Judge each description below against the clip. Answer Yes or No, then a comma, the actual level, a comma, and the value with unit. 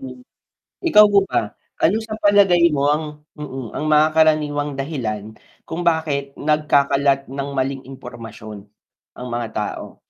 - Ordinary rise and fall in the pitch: Yes, average, 3.3 semitones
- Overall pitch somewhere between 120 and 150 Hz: Yes, medium, 140 Hz